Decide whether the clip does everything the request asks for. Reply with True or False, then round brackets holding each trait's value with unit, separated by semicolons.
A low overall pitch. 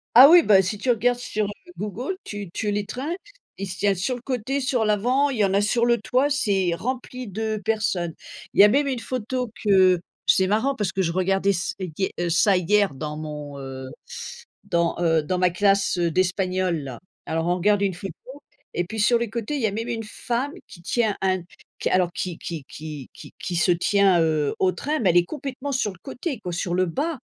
False (200 Hz)